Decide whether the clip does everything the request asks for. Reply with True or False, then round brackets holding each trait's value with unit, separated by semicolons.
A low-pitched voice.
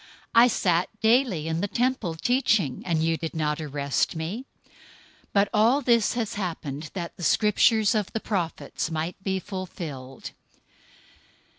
False (185 Hz)